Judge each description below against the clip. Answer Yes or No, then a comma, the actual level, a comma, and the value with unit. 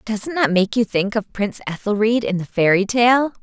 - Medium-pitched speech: No, high, 215 Hz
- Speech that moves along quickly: Yes, fast, 210 wpm